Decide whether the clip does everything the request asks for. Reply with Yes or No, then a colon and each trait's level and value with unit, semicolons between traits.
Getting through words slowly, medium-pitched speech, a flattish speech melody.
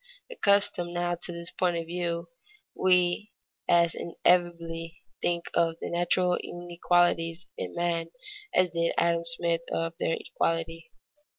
Yes: slow, 125 wpm; medium, 170 Hz; narrow, 0.9 semitones